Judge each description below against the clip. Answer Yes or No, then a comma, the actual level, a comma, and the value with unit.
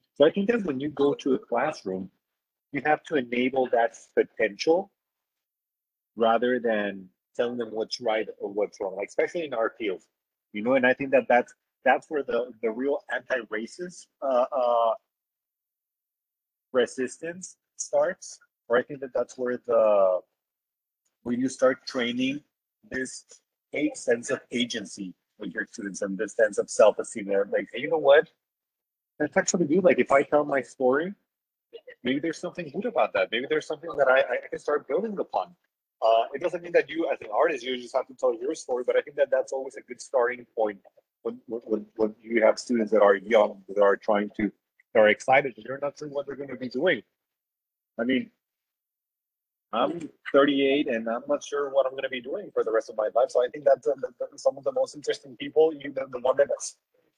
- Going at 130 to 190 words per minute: No, average, 200 wpm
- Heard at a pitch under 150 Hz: Yes, medium, 140 Hz